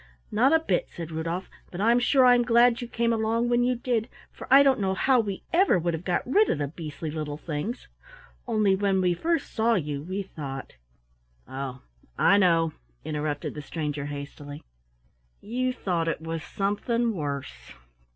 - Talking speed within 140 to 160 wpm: No, average, 180 wpm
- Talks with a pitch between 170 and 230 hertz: Yes, high, 190 Hz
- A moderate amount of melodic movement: No, wide, 7.7 semitones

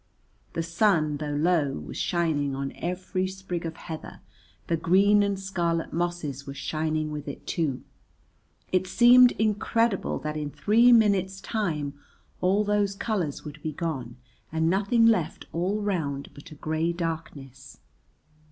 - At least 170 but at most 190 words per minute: No, average, 145 wpm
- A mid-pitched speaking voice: Yes, medium, 170 Hz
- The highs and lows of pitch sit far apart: No, average, 4.6 semitones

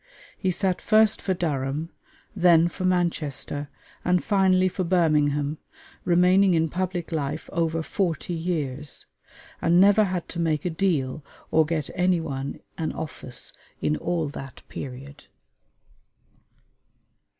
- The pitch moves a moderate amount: Yes, average, 3.5 semitones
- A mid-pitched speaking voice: Yes, medium, 165 Hz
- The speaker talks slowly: Yes, slow, 125 wpm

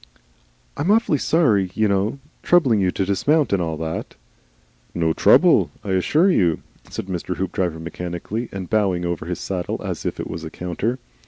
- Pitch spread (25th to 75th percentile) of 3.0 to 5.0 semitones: Yes, average, 4.5 semitones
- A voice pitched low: Yes, very low, 95 Hz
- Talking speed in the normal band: Yes, average, 165 wpm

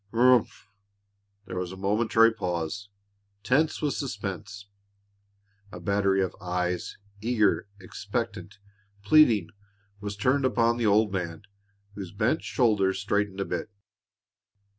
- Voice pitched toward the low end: Yes, low, 100 Hz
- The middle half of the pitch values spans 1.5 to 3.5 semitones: Yes, average, 3.2 semitones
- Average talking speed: No, slow, 115 wpm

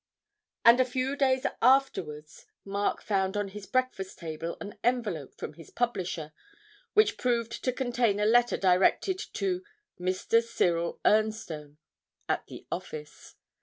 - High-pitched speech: Yes, high, 210 Hz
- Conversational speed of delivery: No, slow, 130 wpm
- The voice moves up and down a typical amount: No, wide, 5.9 semitones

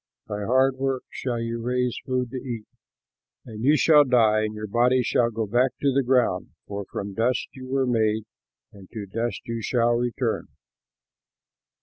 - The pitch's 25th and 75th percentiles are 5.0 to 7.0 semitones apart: No, average, 2.8 semitones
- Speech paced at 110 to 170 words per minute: Yes, average, 165 wpm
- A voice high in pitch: No, low, 120 Hz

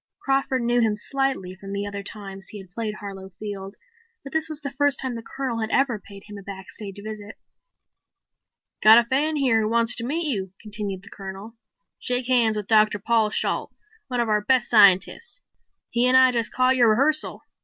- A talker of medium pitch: No, high, 225 Hz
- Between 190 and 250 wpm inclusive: Yes, average, 200 wpm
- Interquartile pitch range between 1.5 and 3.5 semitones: No, average, 4.1 semitones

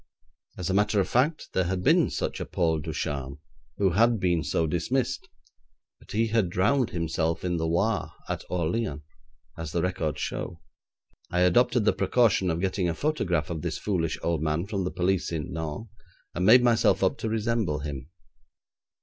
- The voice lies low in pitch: Yes, very low, 90 Hz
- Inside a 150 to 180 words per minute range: Yes, average, 175 wpm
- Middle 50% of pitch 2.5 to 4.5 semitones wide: No, average, 5.0 semitones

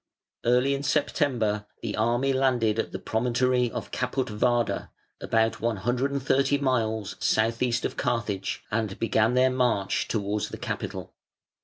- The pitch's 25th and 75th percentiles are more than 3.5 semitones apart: No, average, 2.8 semitones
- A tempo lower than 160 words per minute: Yes, average, 150 wpm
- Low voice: Yes, low, 120 Hz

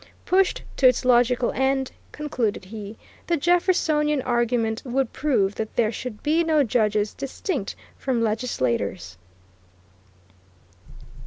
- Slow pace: Yes, slow, 110 wpm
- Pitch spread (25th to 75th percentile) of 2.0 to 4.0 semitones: No, average, 5.1 semitones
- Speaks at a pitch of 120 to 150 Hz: No, high, 245 Hz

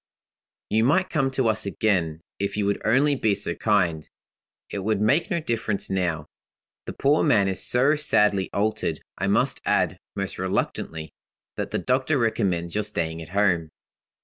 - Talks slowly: No, average, 165 wpm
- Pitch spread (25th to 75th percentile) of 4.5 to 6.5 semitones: Yes, wide, 5.4 semitones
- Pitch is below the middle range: Yes, low, 105 Hz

